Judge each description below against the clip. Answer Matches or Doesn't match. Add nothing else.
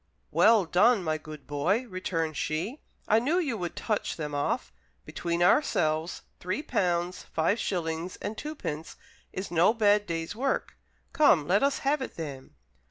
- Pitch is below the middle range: Doesn't match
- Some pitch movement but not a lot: Doesn't match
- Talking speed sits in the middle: Matches